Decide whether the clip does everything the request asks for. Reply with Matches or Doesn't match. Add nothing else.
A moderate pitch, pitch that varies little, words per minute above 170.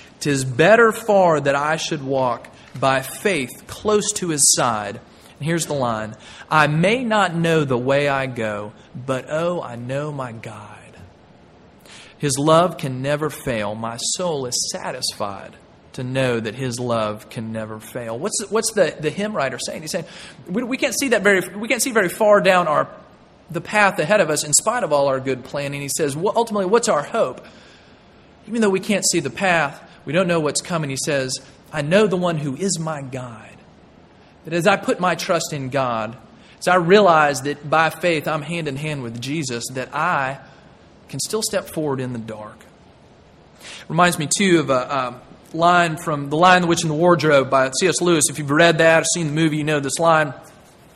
Doesn't match